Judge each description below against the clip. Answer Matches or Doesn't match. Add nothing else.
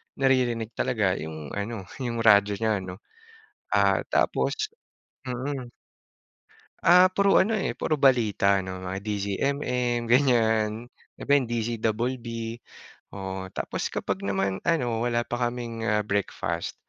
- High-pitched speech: Doesn't match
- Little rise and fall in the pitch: Doesn't match